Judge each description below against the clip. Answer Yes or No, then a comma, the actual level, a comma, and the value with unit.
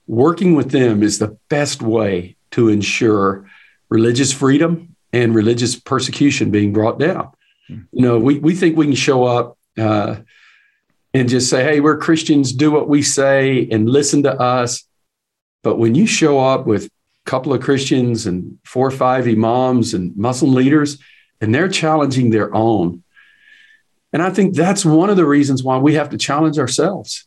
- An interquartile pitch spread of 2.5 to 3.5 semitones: No, average, 4.9 semitones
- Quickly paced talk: No, average, 170 wpm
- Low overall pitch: Yes, low, 130 Hz